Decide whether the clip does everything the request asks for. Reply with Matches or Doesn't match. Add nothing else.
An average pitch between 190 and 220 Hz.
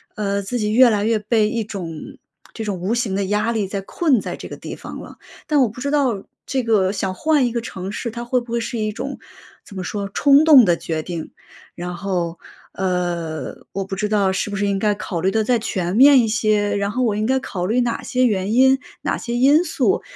Matches